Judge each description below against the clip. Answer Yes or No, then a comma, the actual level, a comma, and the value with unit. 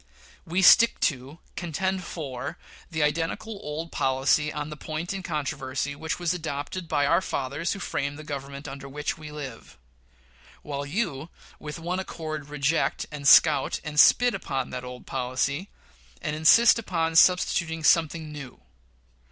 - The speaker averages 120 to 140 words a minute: No, average, 150 wpm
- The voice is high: No, medium, 150 Hz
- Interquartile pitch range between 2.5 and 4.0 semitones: Yes, average, 3.1 semitones